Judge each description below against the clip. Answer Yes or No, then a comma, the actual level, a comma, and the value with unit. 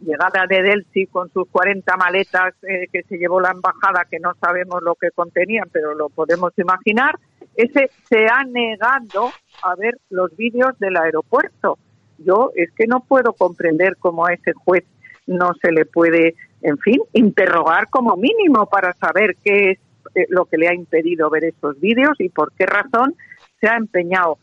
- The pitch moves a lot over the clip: No, average, 3.9 semitones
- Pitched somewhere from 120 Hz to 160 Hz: No, medium, 185 Hz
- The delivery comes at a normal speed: Yes, average, 175 wpm